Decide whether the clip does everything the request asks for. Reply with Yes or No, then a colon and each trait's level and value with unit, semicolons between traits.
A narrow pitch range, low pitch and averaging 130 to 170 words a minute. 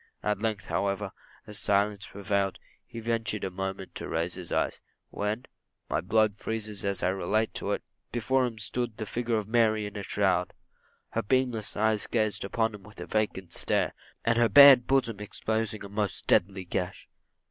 No: narrow, 2.3 semitones; low, 105 Hz; average, 180 wpm